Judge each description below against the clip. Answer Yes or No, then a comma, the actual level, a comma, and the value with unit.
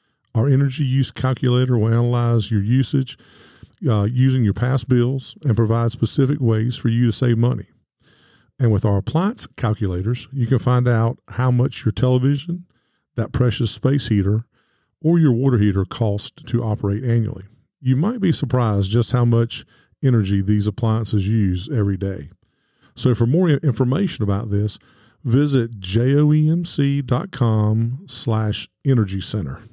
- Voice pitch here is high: No, low, 120 Hz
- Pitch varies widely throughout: No, average, 3.3 semitones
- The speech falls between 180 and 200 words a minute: No, average, 145 wpm